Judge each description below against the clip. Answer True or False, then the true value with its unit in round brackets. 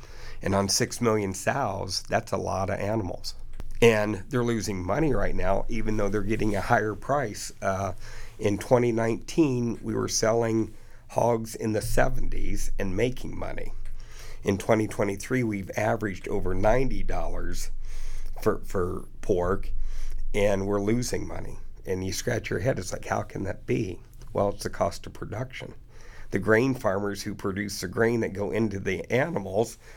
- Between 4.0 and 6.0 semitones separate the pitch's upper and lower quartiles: False (2.7 semitones)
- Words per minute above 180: False (155 wpm)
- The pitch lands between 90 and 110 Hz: True (105 Hz)